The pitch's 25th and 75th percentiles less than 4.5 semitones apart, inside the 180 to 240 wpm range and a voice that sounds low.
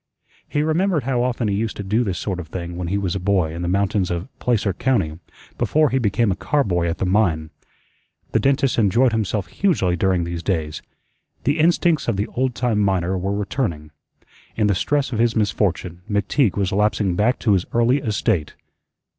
No: average, 5.2 semitones; average, 195 wpm; low, 100 Hz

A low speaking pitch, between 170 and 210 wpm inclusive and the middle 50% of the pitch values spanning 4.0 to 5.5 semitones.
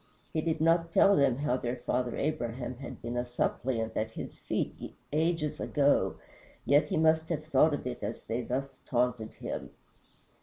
Yes: low, 130 Hz; average, 175 wpm; average, 4.3 semitones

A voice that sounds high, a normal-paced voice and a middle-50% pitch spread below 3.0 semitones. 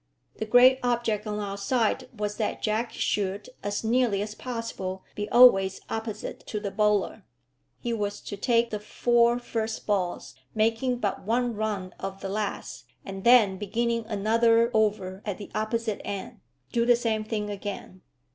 Yes: high, 215 Hz; average, 160 wpm; narrow, 2.5 semitones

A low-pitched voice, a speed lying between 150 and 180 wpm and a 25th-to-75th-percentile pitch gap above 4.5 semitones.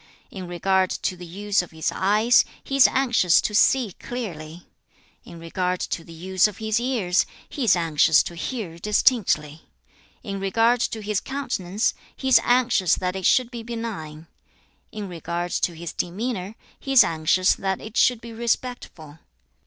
No: high, 195 Hz; average, 165 wpm; average, 5.2 semitones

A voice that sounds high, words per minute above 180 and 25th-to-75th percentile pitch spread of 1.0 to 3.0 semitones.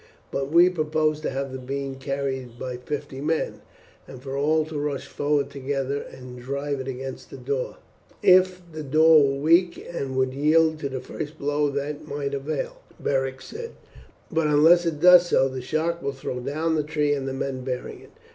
No: medium, 140 Hz; average, 190 wpm; narrow, 2.6 semitones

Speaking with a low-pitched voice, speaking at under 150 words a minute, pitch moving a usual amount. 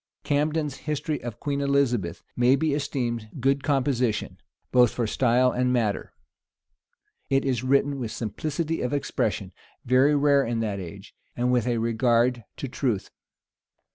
Yes: low, 125 Hz; average, 140 wpm; average, 3.1 semitones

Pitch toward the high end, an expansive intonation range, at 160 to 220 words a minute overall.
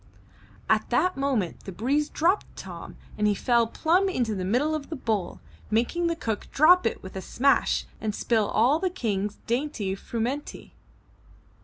Yes: high, 245 Hz; wide, 6.6 semitones; average, 165 wpm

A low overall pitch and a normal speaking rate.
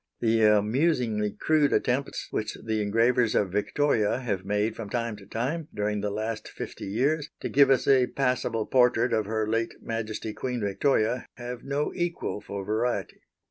Yes: low, 115 Hz; average, 165 wpm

